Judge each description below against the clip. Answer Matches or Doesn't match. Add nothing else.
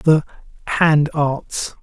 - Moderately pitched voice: Matches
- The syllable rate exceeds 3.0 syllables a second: Doesn't match